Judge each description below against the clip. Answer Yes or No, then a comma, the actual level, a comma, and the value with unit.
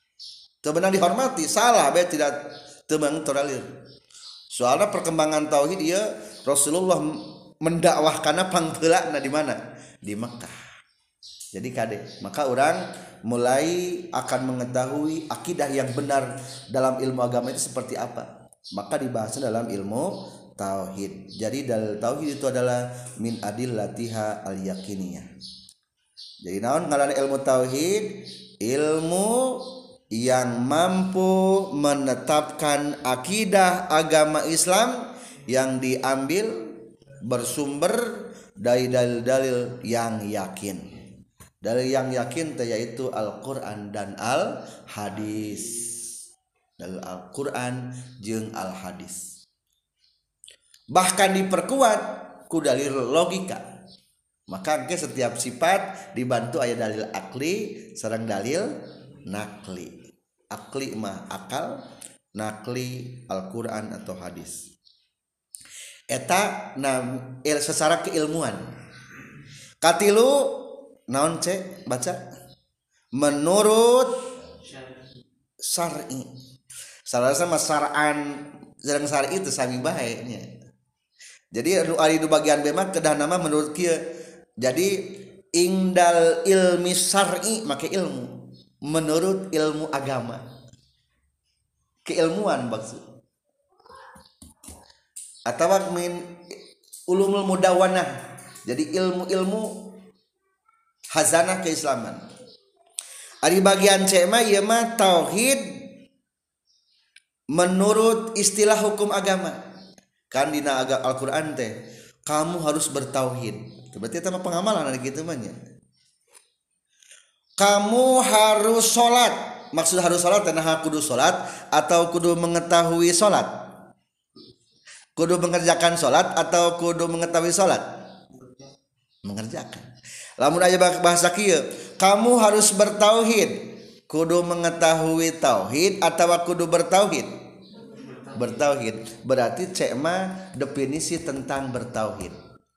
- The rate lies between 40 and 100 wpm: Yes, average, 90 wpm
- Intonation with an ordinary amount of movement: No, wide, 6.8 semitones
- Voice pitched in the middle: Yes, medium, 155 Hz